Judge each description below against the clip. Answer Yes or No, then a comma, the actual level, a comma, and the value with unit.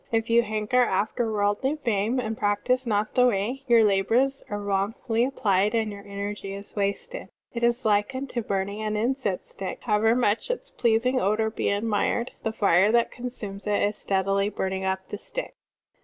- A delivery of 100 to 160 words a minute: No, average, 175 wpm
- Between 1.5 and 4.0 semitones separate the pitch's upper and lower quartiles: Yes, average, 3.0 semitones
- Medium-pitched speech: No, high, 215 Hz